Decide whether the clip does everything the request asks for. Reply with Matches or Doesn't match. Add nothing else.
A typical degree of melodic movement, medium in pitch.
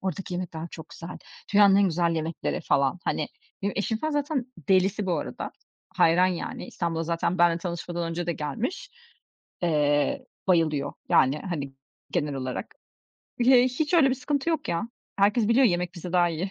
Matches